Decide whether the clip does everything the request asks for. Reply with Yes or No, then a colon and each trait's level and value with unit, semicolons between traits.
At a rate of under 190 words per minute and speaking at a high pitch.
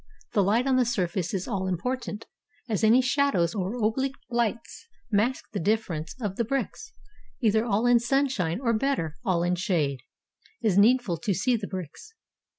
Yes: average, 170 wpm; high, 215 Hz